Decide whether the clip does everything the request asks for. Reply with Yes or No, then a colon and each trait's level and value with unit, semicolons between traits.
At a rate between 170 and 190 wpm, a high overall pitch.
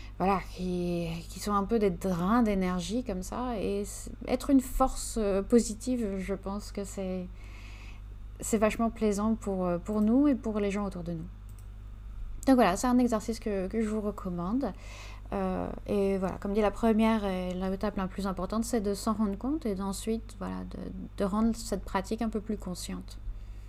Yes: average, 185 wpm; high, 200 Hz